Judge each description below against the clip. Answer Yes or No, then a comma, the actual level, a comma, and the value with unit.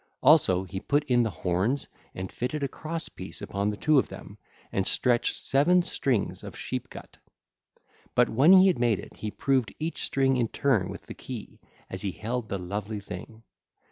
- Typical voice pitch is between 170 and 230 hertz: No, low, 120 Hz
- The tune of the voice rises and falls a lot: Yes, wide, 5.9 semitones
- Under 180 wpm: No, average, 190 wpm